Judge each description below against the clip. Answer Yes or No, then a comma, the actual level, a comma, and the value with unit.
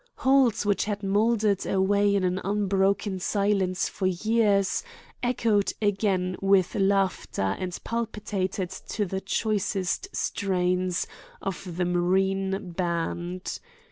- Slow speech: Yes, slow, 110 wpm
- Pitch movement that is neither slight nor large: No, narrow, 1.9 semitones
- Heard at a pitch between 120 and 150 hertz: No, high, 195 Hz